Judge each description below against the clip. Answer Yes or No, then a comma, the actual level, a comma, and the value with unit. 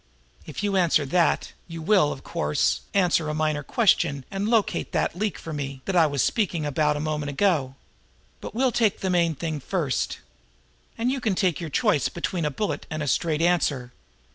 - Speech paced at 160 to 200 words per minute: Yes, average, 190 wpm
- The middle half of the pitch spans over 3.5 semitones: Yes, average, 4.5 semitones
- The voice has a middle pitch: Yes, medium, 165 Hz